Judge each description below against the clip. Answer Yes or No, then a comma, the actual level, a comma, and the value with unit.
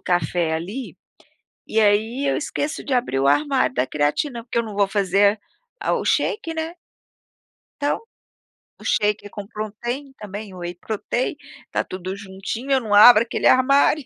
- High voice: Yes, high, 215 Hz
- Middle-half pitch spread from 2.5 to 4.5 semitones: No, average, 5.0 semitones